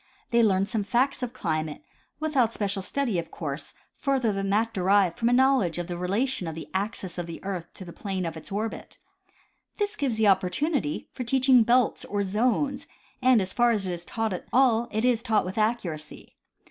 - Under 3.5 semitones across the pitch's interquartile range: No, average, 5.1 semitones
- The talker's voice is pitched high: Yes, high, 215 Hz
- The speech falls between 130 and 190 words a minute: No, average, 200 wpm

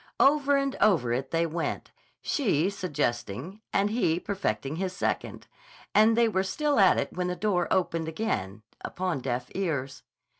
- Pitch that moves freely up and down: Yes, wide, 7.0 semitones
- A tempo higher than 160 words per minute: No, average, 155 wpm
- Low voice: No, medium, 180 Hz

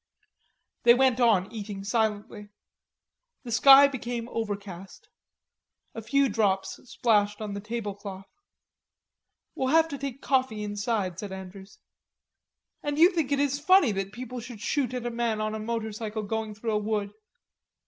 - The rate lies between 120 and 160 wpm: Yes, average, 150 wpm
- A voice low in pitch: No, high, 220 Hz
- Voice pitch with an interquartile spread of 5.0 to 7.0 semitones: No, average, 3.6 semitones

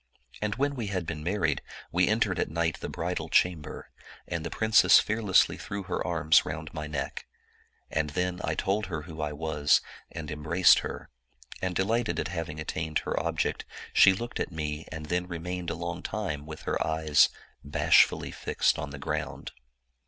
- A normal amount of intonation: Yes, average, 3.3 semitones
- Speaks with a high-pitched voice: No, very low, 85 Hz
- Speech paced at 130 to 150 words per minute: No, average, 180 wpm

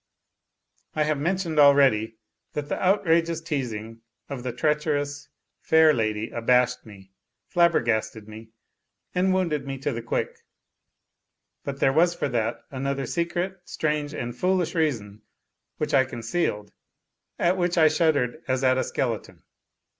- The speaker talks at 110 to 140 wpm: Yes, slow, 135 wpm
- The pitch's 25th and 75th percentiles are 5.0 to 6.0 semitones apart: Yes, wide, 5.5 semitones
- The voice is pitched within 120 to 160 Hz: Yes, medium, 140 Hz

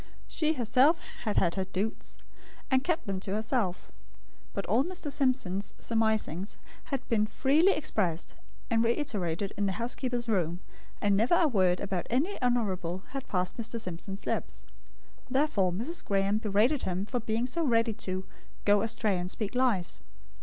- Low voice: No, high, 220 Hz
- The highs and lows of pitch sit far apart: No, average, 5.0 semitones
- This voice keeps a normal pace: Yes, average, 155 wpm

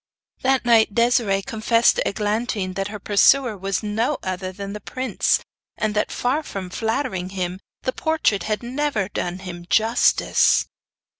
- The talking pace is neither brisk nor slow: Yes, average, 150 wpm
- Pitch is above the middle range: Yes, high, 210 Hz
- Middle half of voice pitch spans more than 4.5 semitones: No, average, 3.8 semitones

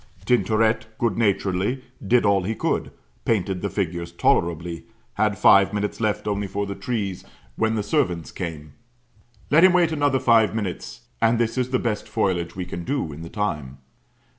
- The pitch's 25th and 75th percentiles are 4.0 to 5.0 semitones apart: Yes, average, 4.3 semitones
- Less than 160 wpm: No, average, 170 wpm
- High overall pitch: No, low, 105 Hz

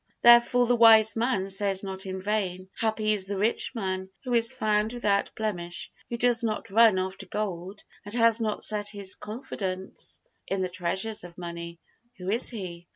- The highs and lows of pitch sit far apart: No, average, 3.1 semitones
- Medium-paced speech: Yes, average, 175 wpm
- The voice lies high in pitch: Yes, high, 205 Hz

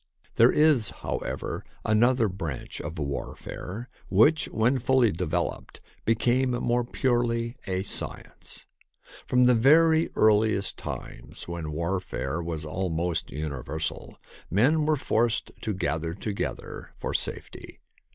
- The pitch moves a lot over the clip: Yes, wide, 6.4 semitones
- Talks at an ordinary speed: No, slow, 115 wpm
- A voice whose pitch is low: Yes, low, 110 Hz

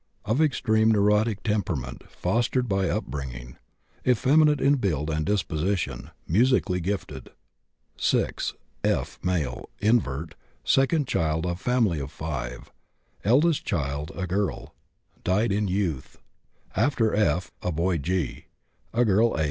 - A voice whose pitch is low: Yes, very low, 95 Hz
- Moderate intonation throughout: No, wide, 6.6 semitones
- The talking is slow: Yes, slow, 120 wpm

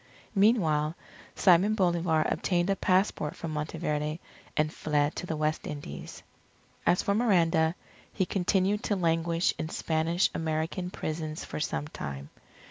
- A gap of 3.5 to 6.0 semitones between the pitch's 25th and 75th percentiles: No, average, 3.1 semitones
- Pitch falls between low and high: Yes, medium, 165 Hz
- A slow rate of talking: Yes, slow, 130 wpm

